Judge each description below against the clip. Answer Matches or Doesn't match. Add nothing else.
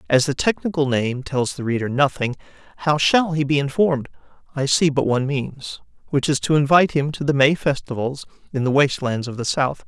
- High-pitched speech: Doesn't match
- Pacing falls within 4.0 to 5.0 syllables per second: Doesn't match